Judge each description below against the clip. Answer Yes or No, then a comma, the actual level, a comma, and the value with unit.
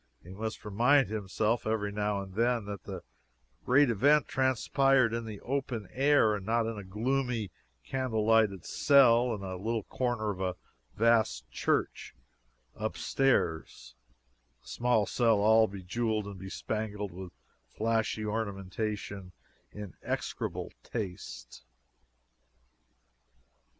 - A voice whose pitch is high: No, low, 110 Hz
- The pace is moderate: No, slow, 120 wpm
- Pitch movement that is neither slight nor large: Yes, average, 3.1 semitones